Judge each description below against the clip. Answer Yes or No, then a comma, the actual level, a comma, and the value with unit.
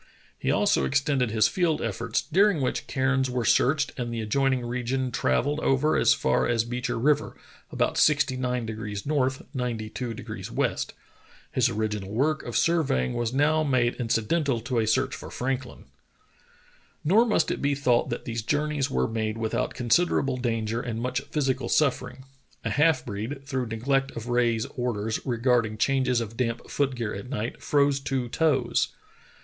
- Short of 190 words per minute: Yes, average, 155 wpm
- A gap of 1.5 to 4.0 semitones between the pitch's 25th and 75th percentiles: Yes, average, 3.3 semitones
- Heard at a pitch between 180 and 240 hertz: No, low, 125 Hz